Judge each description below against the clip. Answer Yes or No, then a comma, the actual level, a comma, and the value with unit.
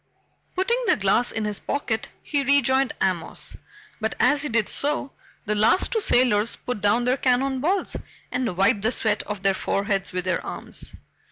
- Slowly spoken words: No, average, 175 wpm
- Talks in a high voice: Yes, high, 230 Hz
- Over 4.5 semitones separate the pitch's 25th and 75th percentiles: Yes, average, 5.0 semitones